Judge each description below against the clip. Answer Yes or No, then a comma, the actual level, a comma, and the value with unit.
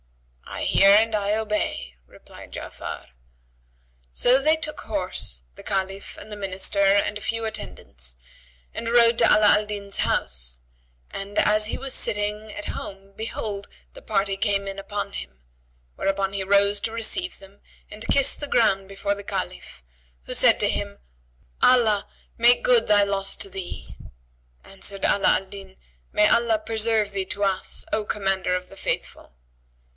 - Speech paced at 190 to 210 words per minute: No, average, 160 wpm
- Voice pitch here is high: Yes, high, 200 Hz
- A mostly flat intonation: Yes, narrow, 1.9 semitones